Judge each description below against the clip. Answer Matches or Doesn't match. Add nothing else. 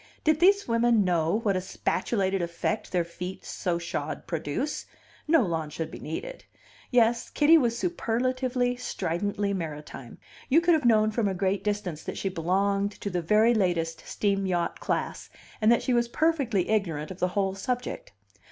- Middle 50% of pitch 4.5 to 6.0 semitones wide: Matches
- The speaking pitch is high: Matches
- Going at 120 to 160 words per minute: Doesn't match